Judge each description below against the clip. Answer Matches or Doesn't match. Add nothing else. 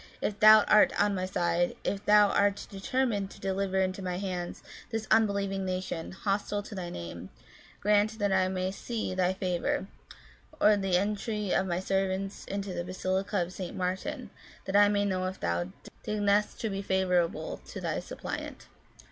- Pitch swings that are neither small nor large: Doesn't match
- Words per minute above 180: Doesn't match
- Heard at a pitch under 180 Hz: Doesn't match